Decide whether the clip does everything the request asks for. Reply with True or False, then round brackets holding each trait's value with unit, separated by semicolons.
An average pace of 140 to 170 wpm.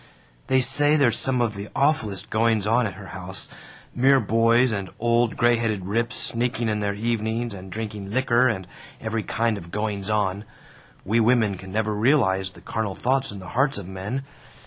False (185 wpm)